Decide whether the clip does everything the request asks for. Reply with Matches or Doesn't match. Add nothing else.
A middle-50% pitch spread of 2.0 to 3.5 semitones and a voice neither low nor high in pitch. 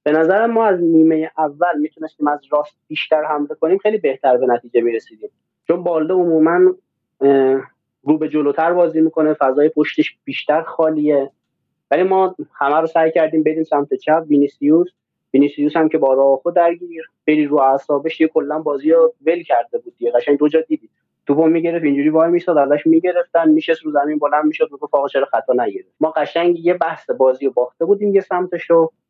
Matches